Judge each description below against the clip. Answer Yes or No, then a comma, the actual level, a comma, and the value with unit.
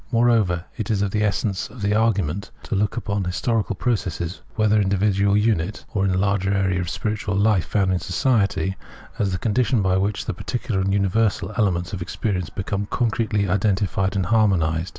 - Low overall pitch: Yes, low, 100 Hz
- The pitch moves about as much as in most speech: No, narrow, 2.3 semitones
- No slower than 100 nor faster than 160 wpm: No, average, 190 wpm